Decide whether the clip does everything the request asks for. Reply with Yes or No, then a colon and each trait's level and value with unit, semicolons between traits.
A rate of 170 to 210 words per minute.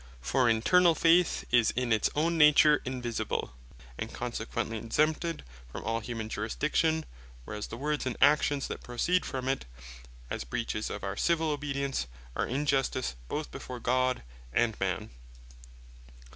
No: average, 140 wpm